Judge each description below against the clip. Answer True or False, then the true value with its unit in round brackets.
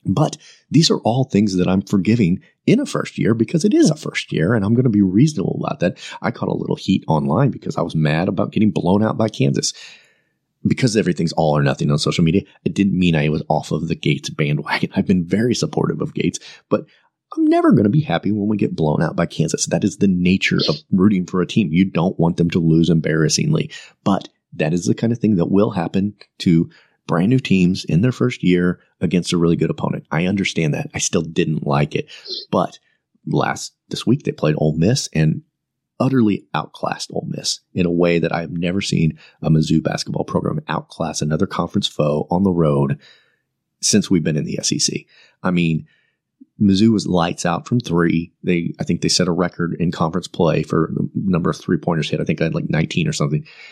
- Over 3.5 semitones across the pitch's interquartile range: True (4.1 semitones)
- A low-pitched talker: True (90 Hz)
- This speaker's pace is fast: True (220 wpm)